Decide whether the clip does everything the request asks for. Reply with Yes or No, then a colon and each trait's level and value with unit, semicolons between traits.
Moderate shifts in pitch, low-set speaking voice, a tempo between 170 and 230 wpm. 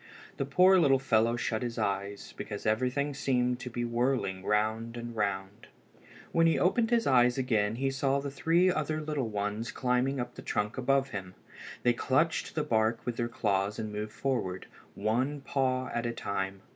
Yes: average, 4.1 semitones; low, 120 Hz; average, 180 wpm